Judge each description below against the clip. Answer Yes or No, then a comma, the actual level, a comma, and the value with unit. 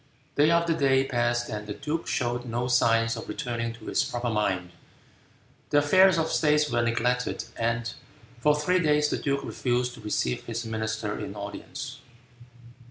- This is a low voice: Yes, low, 120 Hz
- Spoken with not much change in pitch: No, average, 4.2 semitones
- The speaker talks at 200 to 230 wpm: No, average, 165 wpm